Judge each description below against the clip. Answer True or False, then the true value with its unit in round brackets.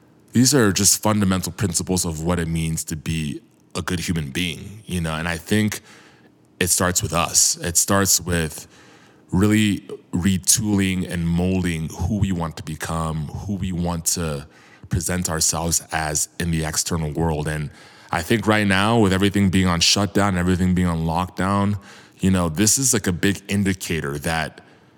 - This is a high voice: False (90 Hz)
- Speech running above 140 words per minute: True (170 wpm)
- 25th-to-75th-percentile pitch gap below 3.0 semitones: False (3.3 semitones)